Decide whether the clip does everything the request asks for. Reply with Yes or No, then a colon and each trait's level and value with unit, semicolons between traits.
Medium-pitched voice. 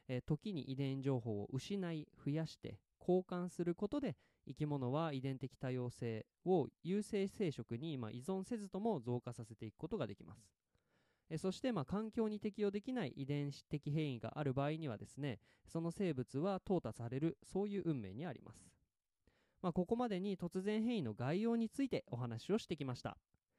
Yes: medium, 150 Hz